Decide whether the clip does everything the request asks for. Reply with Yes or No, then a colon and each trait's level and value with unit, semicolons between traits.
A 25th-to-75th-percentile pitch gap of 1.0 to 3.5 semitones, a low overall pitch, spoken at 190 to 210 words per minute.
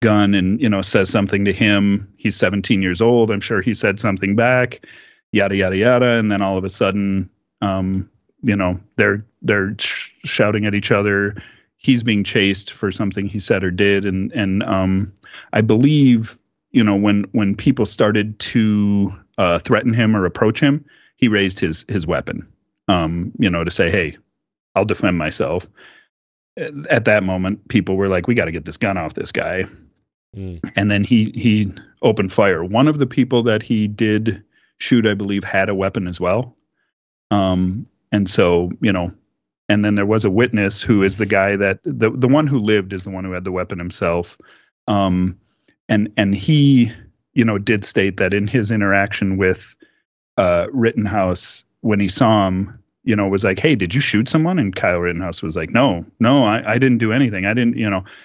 Yes: narrow, 2.6 semitones; low, 100 Hz; average, 195 wpm